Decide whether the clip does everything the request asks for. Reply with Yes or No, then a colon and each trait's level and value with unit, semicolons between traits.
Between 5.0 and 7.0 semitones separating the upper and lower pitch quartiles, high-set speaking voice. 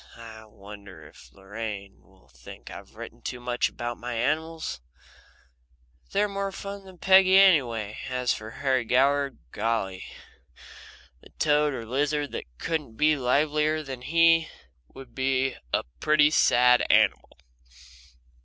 No: average, 5.3 semitones; low, 130 Hz